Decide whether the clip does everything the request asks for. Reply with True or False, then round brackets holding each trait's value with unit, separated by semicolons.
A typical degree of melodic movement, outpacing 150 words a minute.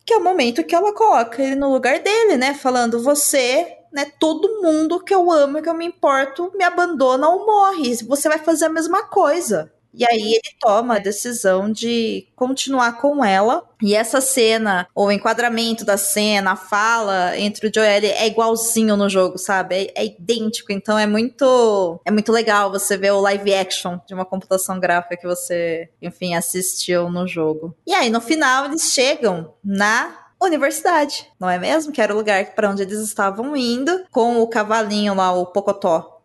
False (6.3 semitones; 185 wpm)